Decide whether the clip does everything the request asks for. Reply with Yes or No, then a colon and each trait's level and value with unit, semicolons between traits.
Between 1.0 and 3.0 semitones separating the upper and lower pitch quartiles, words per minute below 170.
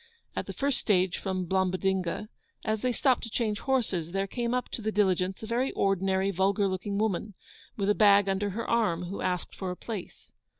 No: average, 2.7 semitones; average, 200 wpm